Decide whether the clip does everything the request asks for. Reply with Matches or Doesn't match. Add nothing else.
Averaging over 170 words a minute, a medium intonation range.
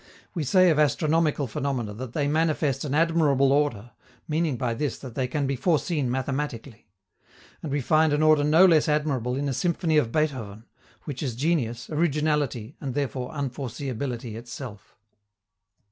Doesn't match